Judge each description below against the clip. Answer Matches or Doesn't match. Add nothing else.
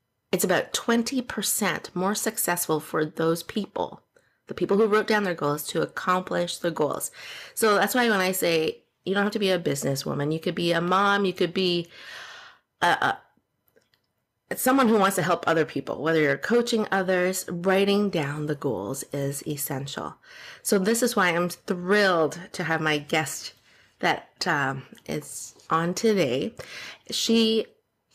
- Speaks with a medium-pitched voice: Matches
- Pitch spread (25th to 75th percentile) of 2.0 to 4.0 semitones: Doesn't match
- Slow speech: Doesn't match